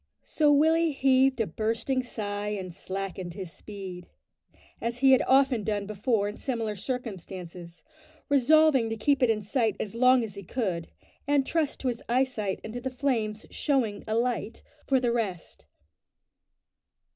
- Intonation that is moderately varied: Yes, average, 4.4 semitones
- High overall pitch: Yes, high, 230 Hz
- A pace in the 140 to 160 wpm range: Yes, average, 155 wpm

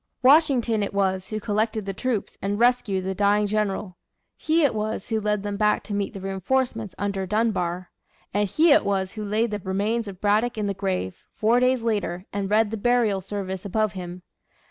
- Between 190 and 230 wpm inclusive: Yes, average, 195 wpm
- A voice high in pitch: Yes, high, 205 Hz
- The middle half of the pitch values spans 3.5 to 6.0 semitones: No, narrow, 2.5 semitones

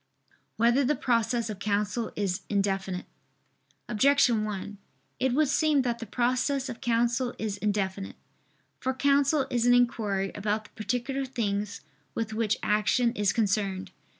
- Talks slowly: No, average, 145 wpm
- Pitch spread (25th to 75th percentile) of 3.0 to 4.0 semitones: Yes, average, 3.6 semitones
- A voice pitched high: Yes, high, 230 Hz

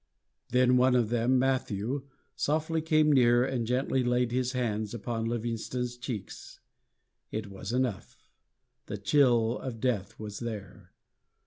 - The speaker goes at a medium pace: No, slow, 130 wpm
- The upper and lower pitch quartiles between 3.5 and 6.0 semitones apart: No, narrow, 2.4 semitones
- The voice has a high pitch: No, low, 120 Hz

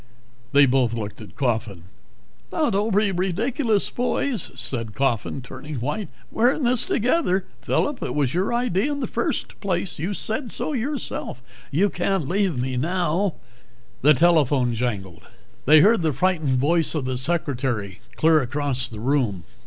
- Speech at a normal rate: Yes, average, 160 wpm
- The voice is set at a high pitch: No, medium, 150 Hz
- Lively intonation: Yes, wide, 8.1 semitones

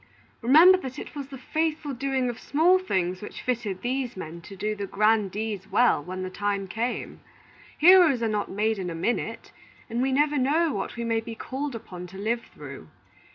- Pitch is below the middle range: No, high, 230 Hz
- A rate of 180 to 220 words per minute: Yes, average, 200 wpm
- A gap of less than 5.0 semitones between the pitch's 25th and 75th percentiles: No, wide, 5.6 semitones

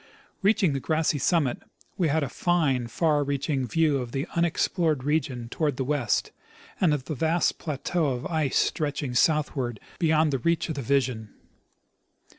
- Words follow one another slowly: No, average, 160 wpm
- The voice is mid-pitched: Yes, medium, 145 Hz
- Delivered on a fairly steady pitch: No, average, 3.4 semitones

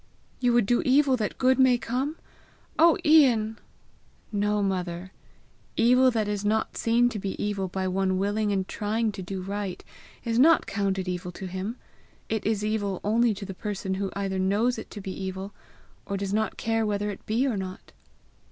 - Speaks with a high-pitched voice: Yes, high, 205 Hz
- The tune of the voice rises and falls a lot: No, average, 3.1 semitones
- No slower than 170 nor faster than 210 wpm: Yes, average, 185 wpm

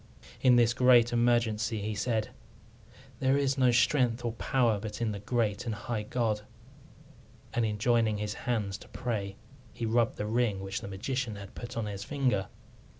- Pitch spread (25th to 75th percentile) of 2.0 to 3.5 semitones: Yes, narrow, 2.6 semitones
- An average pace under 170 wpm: No, average, 175 wpm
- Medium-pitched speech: No, low, 115 Hz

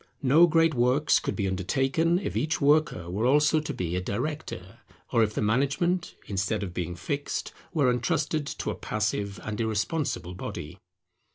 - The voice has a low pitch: Yes, low, 125 Hz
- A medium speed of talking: Yes, average, 165 wpm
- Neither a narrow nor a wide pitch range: No, wide, 7.4 semitones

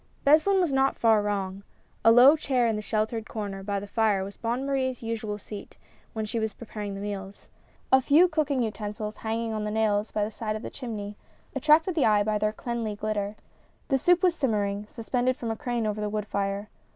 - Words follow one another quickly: Yes, fast, 210 wpm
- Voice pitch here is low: No, high, 220 Hz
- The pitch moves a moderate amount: Yes, average, 3.4 semitones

